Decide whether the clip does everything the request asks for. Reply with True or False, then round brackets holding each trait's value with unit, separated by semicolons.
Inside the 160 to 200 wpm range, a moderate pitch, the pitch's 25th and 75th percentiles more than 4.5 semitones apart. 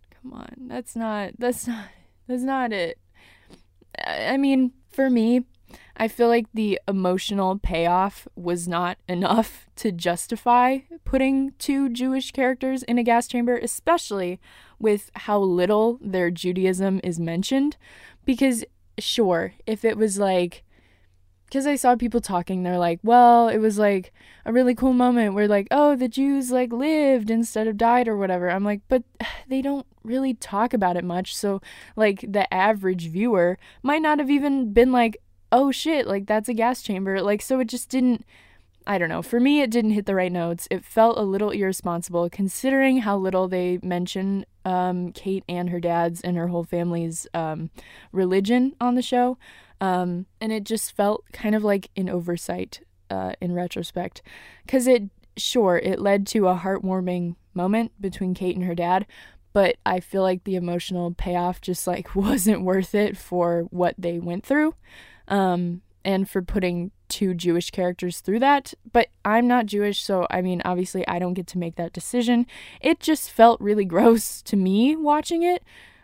False (170 wpm; 205 Hz; 5.3 semitones)